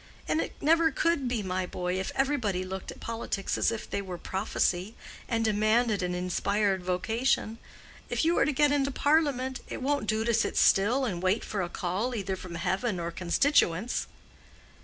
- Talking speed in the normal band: Yes, average, 180 wpm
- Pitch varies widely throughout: Yes, wide, 5.9 semitones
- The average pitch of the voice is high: Yes, high, 215 Hz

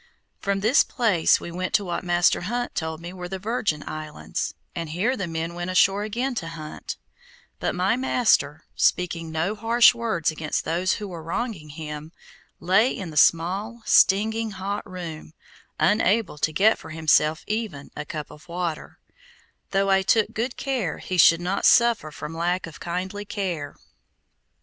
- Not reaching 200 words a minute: Yes, average, 165 wpm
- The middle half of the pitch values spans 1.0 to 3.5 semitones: No, average, 4.6 semitones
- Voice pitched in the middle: Yes, medium, 180 Hz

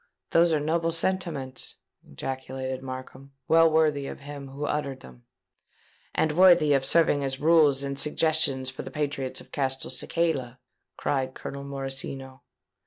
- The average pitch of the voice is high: No, medium, 140 Hz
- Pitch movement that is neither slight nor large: Yes, average, 3.0 semitones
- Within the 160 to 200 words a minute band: No, average, 140 wpm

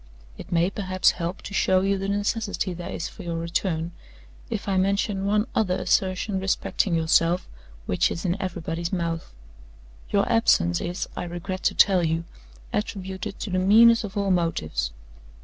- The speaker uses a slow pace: No, average, 165 wpm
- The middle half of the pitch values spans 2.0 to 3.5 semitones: Yes, average, 2.8 semitones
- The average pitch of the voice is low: No, medium, 185 Hz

